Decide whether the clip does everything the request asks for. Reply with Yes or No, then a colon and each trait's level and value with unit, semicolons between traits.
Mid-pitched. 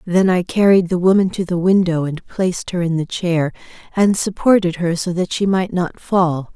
Yes: medium, 180 Hz